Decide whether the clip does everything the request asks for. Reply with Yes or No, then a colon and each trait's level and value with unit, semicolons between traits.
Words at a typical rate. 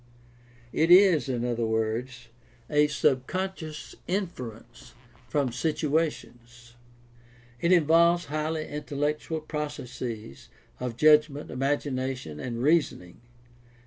No: slow, 90 wpm